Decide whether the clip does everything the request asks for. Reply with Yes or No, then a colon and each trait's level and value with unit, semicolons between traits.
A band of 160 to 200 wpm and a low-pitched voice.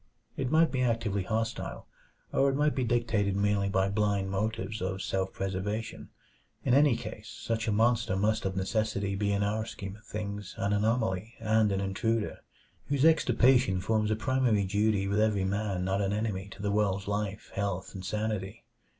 Yes: average, 175 wpm; low, 105 Hz